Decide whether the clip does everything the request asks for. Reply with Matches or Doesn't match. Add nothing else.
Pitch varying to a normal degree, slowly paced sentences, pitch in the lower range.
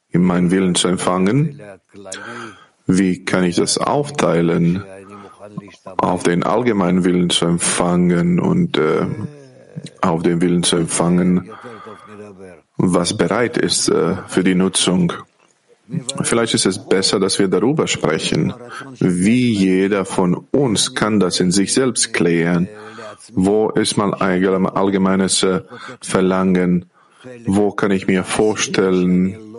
Matches